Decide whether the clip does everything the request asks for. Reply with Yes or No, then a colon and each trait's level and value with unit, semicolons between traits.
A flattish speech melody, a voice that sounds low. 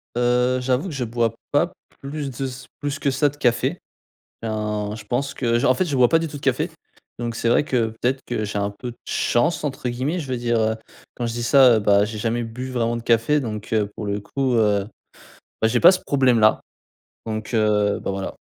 No: average, 3.3 semitones; low, 120 Hz